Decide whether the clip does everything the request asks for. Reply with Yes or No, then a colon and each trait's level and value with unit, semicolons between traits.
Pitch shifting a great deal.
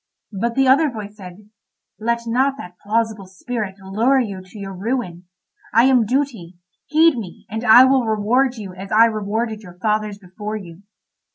No: average, 3.8 semitones